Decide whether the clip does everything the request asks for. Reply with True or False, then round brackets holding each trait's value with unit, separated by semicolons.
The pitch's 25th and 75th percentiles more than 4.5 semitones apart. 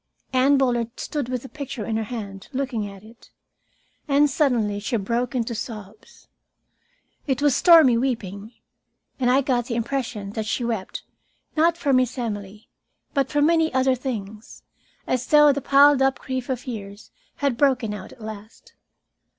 False (3.9 semitones)